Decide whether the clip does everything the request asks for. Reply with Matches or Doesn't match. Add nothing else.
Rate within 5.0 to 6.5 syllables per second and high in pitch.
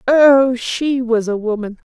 Doesn't match